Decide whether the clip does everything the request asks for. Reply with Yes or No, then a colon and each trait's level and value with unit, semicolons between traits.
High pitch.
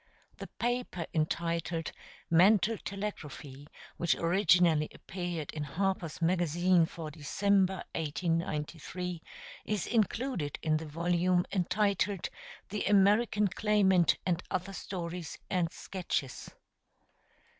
No: medium, 175 Hz